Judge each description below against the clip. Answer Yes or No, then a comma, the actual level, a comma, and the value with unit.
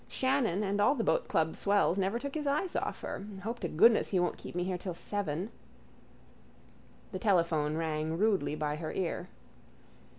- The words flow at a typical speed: Yes, average, 170 wpm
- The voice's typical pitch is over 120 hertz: Yes, high, 190 Hz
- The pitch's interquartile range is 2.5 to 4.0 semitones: No, average, 5.1 semitones